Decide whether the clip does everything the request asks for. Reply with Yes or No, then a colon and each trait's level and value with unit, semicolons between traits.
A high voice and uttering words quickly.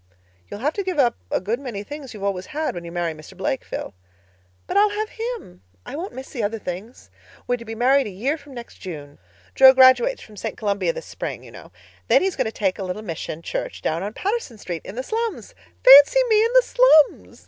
Yes: high, 245 Hz; fast, 230 wpm